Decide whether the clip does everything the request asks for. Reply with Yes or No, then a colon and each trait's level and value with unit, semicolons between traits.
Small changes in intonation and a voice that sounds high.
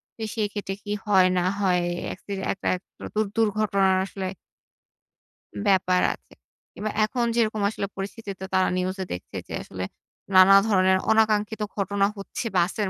Yes: narrow, 2.3 semitones; high, 200 Hz